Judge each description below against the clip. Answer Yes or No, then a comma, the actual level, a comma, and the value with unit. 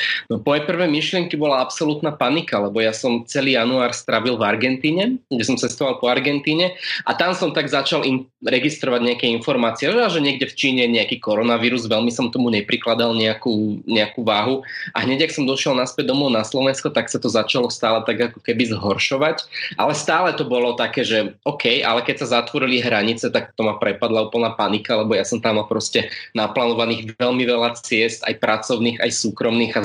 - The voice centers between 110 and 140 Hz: Yes, low, 125 Hz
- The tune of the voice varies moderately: Yes, average, 3.9 semitones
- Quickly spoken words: Yes, fast, 185 wpm